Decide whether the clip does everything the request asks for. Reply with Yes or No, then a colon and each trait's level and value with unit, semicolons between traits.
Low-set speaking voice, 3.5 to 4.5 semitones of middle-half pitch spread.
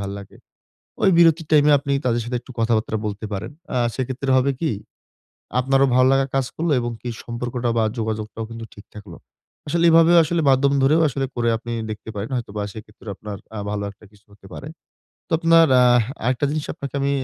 Yes: low, 125 Hz; average, 4.2 semitones